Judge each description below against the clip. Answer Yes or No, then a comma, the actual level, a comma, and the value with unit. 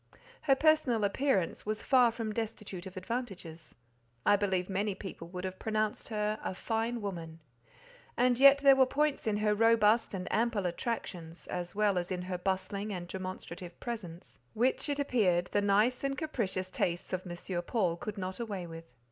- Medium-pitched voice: No, high, 205 Hz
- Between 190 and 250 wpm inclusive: No, average, 175 wpm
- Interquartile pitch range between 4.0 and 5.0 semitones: Yes, average, 4.3 semitones